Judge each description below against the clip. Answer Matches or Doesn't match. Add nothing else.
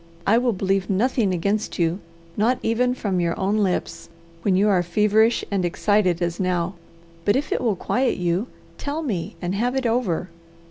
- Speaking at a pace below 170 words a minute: Doesn't match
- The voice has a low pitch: Doesn't match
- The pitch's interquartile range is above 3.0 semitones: Matches